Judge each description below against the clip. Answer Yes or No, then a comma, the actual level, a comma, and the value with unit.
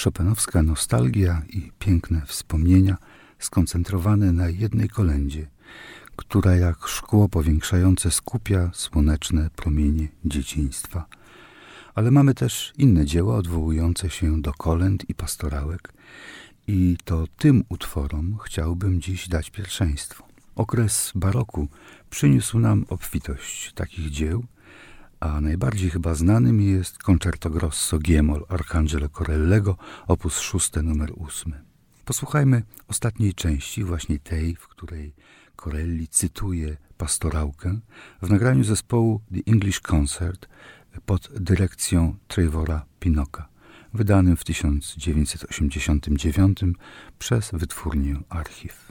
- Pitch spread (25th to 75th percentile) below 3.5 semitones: No, average, 4.0 semitones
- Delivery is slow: Yes, slow, 100 wpm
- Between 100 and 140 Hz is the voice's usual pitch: No, very low, 90 Hz